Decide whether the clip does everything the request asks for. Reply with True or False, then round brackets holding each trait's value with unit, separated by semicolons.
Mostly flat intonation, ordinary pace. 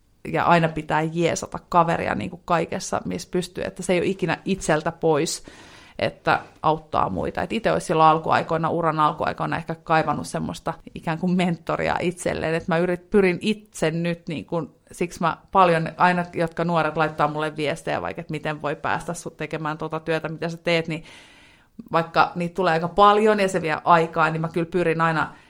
False (2.0 semitones; 185 wpm)